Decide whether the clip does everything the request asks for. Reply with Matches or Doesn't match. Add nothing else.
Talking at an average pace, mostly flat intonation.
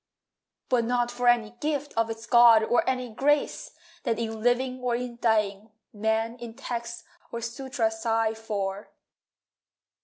Matches